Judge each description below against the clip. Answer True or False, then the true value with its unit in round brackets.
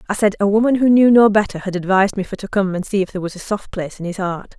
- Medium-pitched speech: False (200 Hz)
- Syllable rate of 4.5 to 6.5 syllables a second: False (7.1 syllables/s)